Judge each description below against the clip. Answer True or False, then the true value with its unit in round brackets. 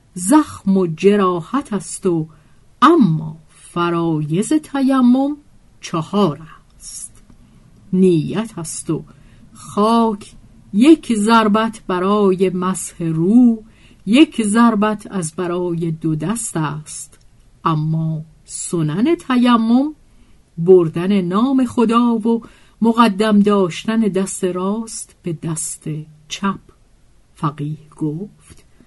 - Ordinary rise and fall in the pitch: False (5.8 semitones)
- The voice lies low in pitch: False (190 Hz)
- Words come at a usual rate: False (85 wpm)